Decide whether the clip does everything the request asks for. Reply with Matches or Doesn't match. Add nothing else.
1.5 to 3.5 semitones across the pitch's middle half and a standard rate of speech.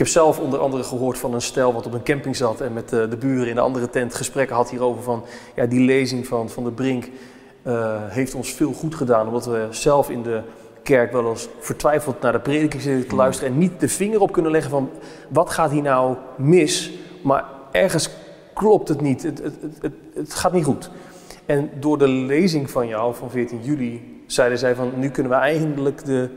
Doesn't match